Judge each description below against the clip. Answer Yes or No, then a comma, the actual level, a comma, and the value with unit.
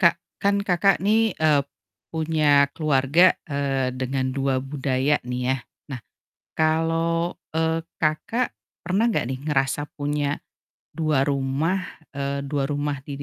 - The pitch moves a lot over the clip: No, average, 3.2 semitones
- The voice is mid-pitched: Yes, medium, 150 Hz